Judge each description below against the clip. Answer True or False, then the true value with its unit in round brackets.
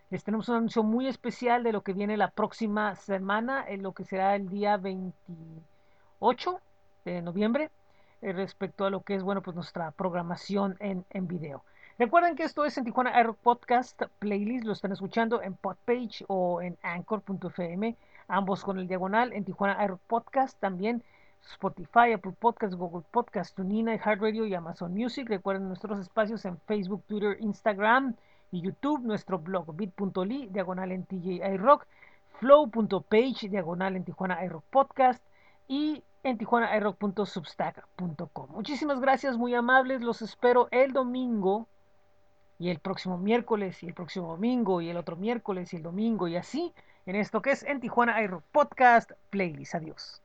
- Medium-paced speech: True (155 wpm)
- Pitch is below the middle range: False (205 Hz)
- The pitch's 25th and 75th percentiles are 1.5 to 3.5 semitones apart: False (4.1 semitones)